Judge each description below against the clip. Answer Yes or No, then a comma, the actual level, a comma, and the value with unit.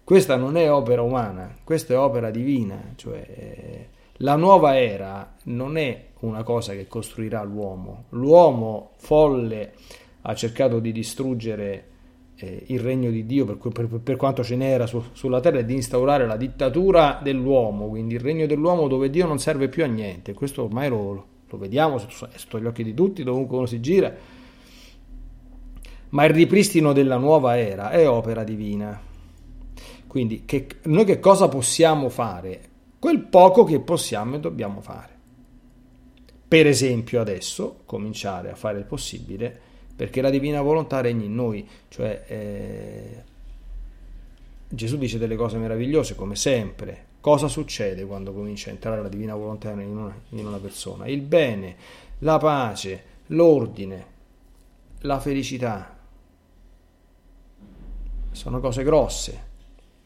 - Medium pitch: No, low, 120 Hz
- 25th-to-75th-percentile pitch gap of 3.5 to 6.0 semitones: Yes, average, 5.1 semitones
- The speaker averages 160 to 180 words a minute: No, average, 145 wpm